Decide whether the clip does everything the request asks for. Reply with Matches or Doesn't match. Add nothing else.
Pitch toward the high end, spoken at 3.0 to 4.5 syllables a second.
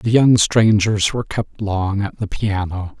Doesn't match